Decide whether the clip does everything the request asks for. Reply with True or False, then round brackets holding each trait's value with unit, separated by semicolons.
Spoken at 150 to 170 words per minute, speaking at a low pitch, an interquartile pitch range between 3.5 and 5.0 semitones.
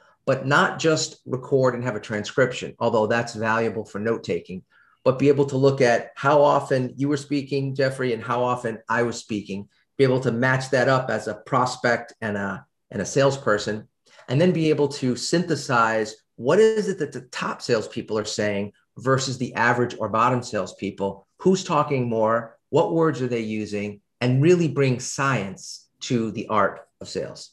False (180 wpm; 125 Hz; 3.9 semitones)